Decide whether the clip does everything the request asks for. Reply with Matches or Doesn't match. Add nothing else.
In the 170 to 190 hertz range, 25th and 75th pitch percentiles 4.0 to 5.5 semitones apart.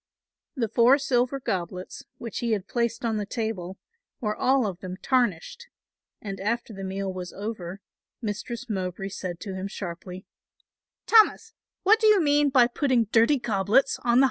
Doesn't match